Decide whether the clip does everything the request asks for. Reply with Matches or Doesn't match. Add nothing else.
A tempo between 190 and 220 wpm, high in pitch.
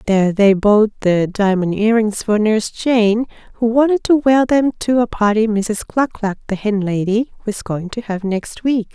Matches